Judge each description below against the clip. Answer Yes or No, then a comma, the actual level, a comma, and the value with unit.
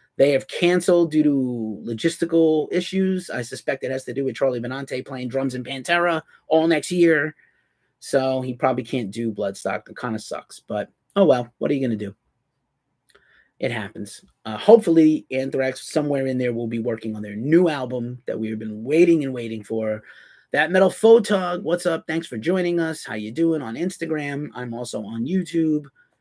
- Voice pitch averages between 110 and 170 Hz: Yes, medium, 140 Hz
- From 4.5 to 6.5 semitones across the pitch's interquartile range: Yes, average, 5.1 semitones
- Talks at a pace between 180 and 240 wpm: Yes, average, 190 wpm